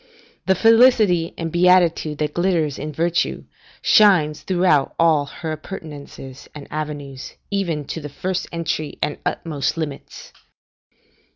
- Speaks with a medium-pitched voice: Yes, medium, 160 Hz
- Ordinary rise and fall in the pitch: Yes, average, 3.3 semitones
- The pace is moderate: No, slow, 120 wpm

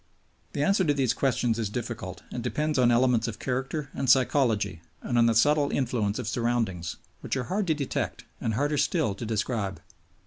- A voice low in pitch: Yes, low, 125 Hz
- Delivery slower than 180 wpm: No, average, 185 wpm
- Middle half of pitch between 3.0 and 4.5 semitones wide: Yes, average, 4.1 semitones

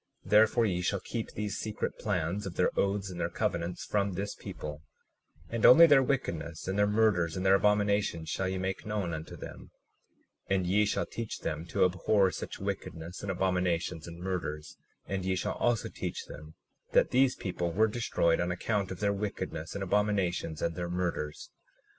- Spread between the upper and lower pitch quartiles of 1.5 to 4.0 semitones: Yes, average, 3.2 semitones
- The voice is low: Yes, very low, 95 Hz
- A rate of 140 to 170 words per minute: No, average, 185 wpm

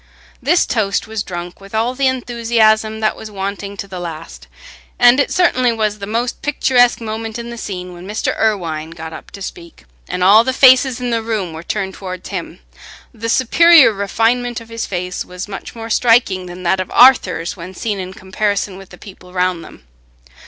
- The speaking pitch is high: Yes, high, 210 Hz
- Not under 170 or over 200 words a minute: Yes, average, 195 wpm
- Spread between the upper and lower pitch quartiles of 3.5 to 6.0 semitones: Yes, average, 4.2 semitones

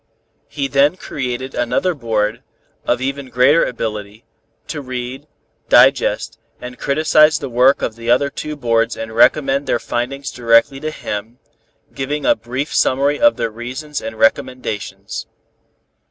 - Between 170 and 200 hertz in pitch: No, low, 130 Hz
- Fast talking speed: No, average, 140 wpm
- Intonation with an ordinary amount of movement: Yes, average, 3.3 semitones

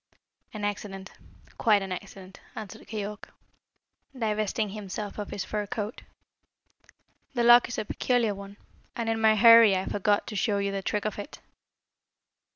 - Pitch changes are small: Yes, narrow, 1.7 semitones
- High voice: Yes, high, 210 Hz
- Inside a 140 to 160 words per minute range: Yes, average, 155 wpm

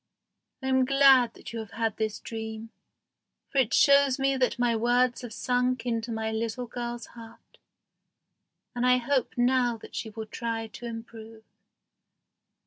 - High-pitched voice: Yes, high, 240 Hz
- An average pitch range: No, narrow, 2.0 semitones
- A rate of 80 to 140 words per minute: No, average, 155 wpm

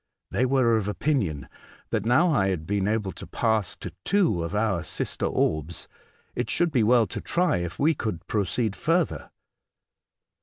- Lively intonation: Yes, wide, 5.8 semitones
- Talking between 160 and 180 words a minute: Yes, average, 165 wpm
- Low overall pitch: Yes, low, 110 Hz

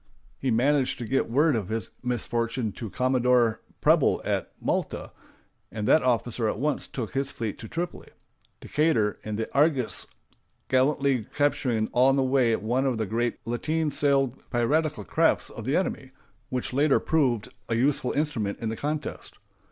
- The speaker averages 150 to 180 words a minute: Yes, average, 155 wpm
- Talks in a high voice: No, low, 130 Hz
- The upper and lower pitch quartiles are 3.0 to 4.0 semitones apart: Yes, average, 3.7 semitones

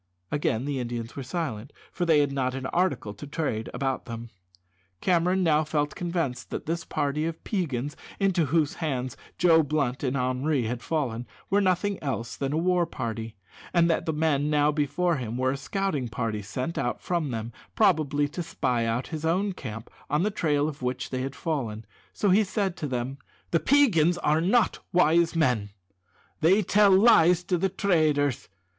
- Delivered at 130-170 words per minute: No, average, 185 wpm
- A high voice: No, medium, 150 Hz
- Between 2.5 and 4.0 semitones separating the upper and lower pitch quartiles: No, average, 5.2 semitones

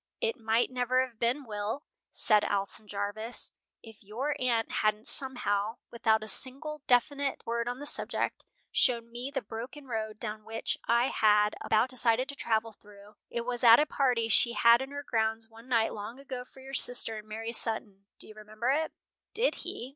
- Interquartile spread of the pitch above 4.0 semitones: No, average, 2.9 semitones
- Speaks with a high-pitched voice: Yes, high, 235 Hz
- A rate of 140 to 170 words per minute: No, average, 185 wpm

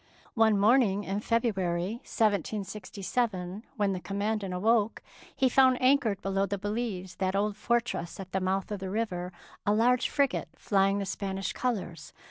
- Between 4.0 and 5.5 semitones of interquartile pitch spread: No, average, 3.1 semitones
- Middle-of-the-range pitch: No, high, 205 Hz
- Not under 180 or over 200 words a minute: No, average, 150 wpm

